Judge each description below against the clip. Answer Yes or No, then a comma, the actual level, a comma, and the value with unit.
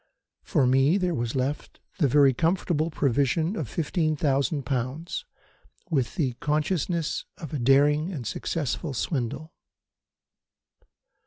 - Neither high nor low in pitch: Yes, medium, 150 Hz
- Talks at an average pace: No, slow, 110 wpm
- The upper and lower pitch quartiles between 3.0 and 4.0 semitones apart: Yes, average, 3.5 semitones